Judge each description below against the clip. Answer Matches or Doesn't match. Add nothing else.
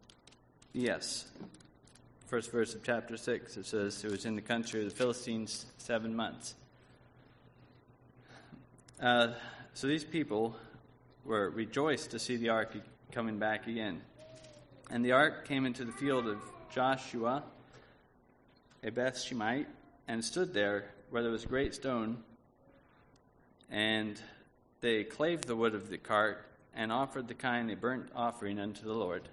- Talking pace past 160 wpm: Doesn't match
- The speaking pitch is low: Matches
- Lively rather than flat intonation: Doesn't match